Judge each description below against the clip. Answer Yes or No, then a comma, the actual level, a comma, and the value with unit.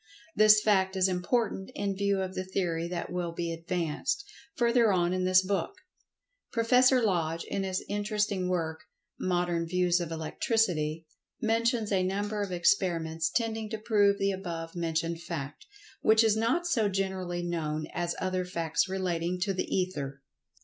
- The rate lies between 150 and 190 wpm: Yes, average, 155 wpm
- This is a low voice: No, medium, 185 Hz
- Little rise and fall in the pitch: No, average, 3.4 semitones